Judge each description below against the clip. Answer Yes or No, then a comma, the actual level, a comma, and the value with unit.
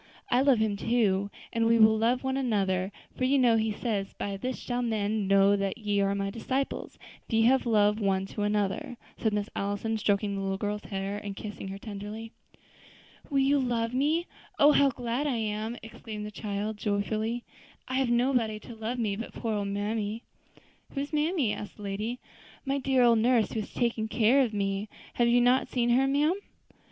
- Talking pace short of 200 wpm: No, fast, 205 wpm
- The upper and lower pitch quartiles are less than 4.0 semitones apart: Yes, average, 3.2 semitones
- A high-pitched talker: Yes, high, 220 Hz